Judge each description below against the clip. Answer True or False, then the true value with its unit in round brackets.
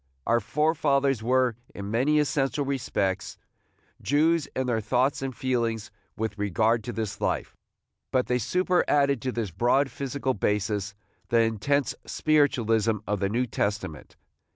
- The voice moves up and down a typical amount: True (4.3 semitones)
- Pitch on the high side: False (125 Hz)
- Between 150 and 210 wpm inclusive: False (140 wpm)